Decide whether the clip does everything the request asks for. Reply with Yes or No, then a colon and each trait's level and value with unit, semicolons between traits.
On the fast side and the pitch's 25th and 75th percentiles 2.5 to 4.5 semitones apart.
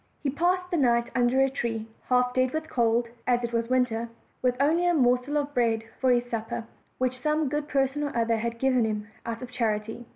Yes: fast, 215 wpm; average, 3.0 semitones